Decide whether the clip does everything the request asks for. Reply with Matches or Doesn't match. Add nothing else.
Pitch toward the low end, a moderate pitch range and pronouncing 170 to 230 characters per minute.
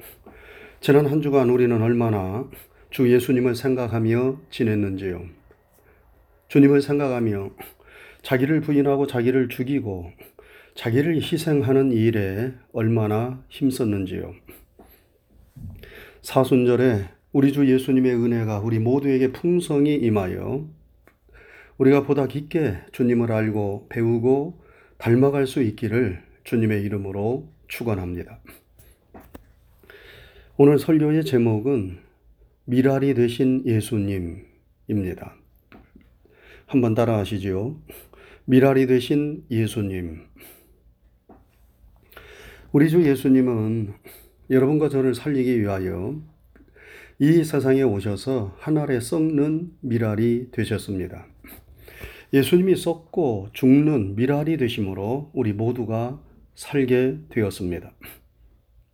Matches